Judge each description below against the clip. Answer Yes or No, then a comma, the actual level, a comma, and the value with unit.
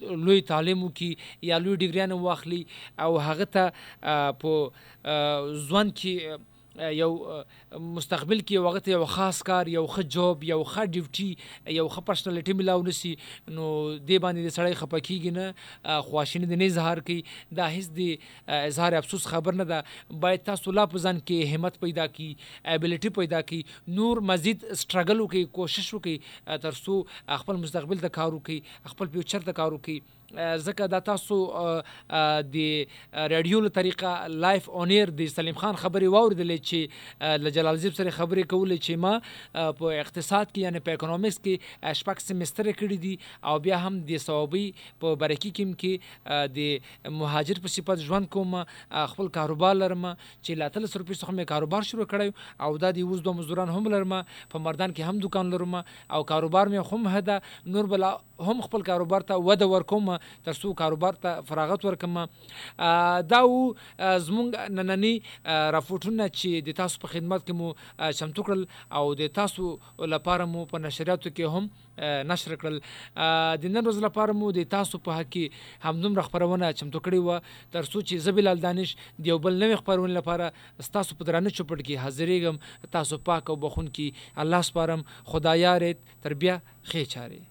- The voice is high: No, medium, 175 Hz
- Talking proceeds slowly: No, average, 145 wpm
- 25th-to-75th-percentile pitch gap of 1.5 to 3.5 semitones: Yes, average, 3.2 semitones